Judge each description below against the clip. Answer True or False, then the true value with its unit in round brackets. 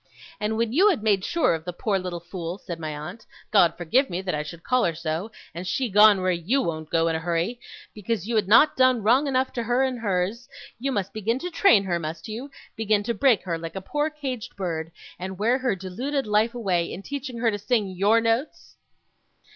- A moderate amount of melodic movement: False (5.7 semitones)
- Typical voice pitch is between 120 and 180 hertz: False (210 Hz)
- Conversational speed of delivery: False (225 wpm)